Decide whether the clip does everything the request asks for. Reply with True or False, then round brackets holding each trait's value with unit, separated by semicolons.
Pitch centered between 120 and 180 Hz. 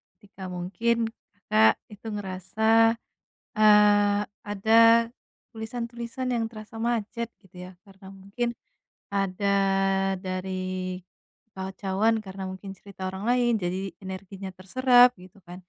False (200 Hz)